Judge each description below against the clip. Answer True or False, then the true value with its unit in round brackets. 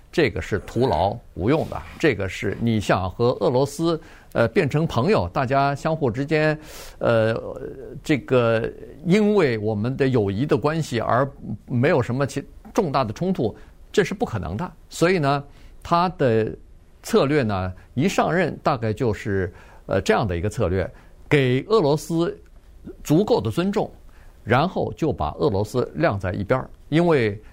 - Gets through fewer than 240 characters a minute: True (225 characters per minute)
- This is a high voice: False (135 Hz)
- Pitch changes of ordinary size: False (6.0 semitones)